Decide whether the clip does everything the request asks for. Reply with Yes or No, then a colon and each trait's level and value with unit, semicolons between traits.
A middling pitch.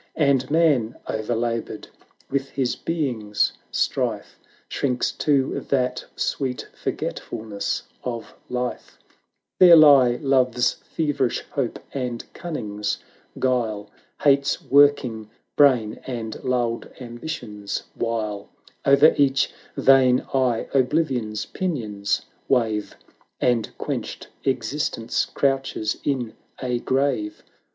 No: low, 125 Hz